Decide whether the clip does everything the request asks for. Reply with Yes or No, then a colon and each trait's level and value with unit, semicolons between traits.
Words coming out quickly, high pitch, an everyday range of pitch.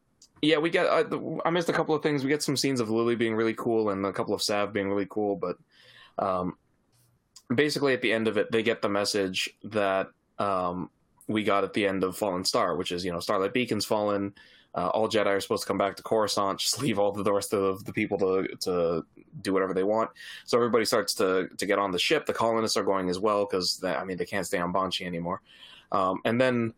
No: fast, 240 wpm; low, 105 Hz; average, 3.1 semitones